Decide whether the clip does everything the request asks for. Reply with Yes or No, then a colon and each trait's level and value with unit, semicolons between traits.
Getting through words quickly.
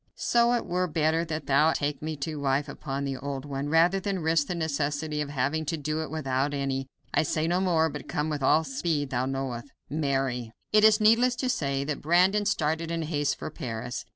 Yes: fast, 215 wpm